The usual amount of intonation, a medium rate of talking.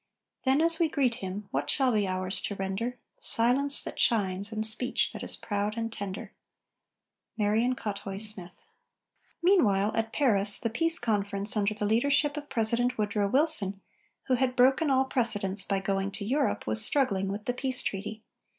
Yes: average, 4.3 semitones; average, 170 wpm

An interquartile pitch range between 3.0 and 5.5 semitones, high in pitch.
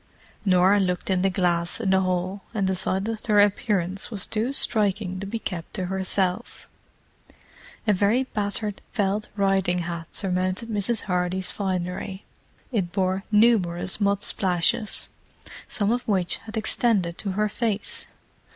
No: narrow, 2.5 semitones; high, 195 Hz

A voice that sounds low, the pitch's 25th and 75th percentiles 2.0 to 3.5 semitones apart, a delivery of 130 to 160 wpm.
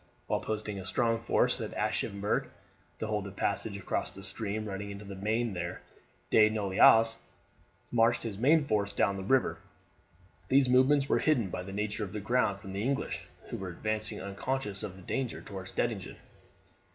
No: low, 105 Hz; average, 2.7 semitones; average, 175 wpm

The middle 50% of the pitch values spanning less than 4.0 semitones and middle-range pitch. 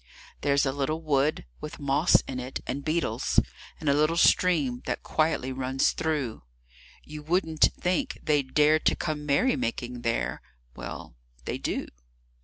Yes: average, 2.9 semitones; medium, 150 Hz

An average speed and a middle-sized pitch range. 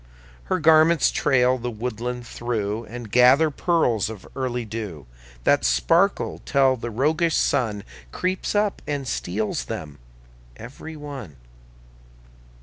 No: slow, 120 wpm; average, 5.0 semitones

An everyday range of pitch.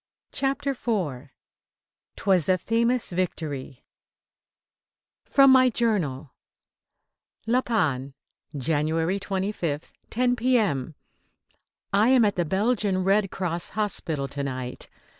No: wide, 7.4 semitones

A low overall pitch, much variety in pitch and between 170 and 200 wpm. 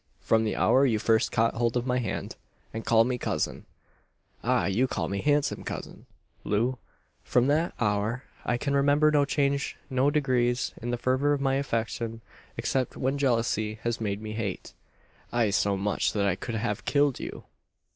No: low, 120 Hz; average, 3.8 semitones; average, 175 wpm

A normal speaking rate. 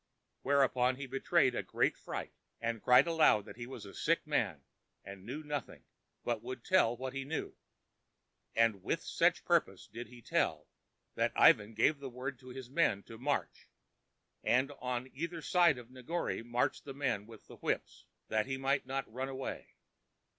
Yes: average, 175 wpm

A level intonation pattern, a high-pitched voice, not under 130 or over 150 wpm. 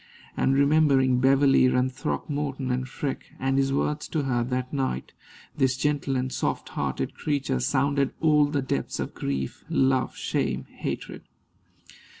No: narrow, 1.7 semitones; low, 135 Hz; average, 145 wpm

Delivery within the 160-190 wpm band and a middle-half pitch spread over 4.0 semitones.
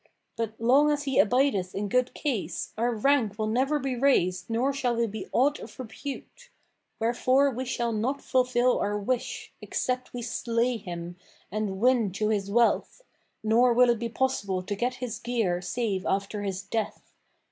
No: average, 170 wpm; average, 3.6 semitones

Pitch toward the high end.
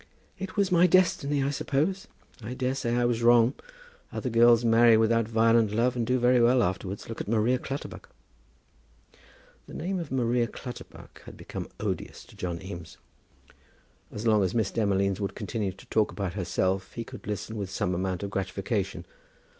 No: low, 115 Hz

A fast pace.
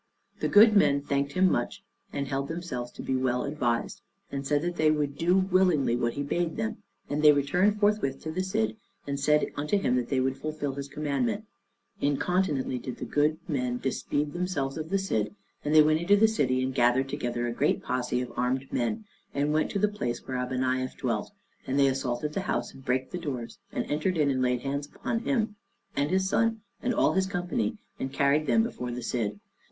Yes: fast, 210 wpm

